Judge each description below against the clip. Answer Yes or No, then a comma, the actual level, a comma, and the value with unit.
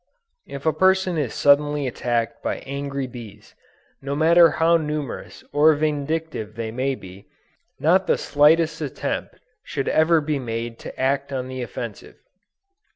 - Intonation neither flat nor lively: Yes, average, 3.7 semitones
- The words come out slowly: No, average, 145 wpm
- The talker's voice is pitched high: No, medium, 140 Hz